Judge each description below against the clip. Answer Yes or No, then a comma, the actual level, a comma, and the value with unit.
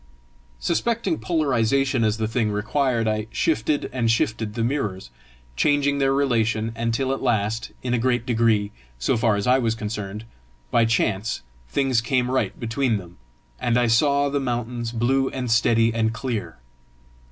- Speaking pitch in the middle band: No, low, 115 Hz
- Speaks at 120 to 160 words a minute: Yes, average, 155 wpm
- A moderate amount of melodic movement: Yes, average, 3.1 semitones